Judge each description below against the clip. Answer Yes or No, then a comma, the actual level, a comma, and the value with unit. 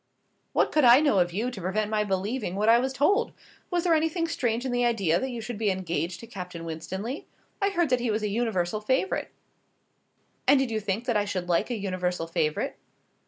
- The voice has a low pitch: No, high, 215 Hz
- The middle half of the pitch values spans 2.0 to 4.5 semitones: No, average, 5.3 semitones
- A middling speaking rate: No, fast, 215 wpm